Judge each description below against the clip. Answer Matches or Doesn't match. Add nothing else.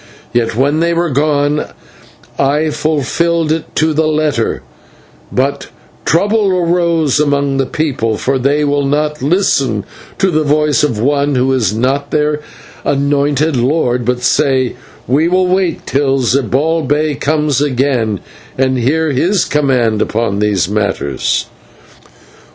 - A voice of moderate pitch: Matches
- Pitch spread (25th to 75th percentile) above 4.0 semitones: Doesn't match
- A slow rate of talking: Matches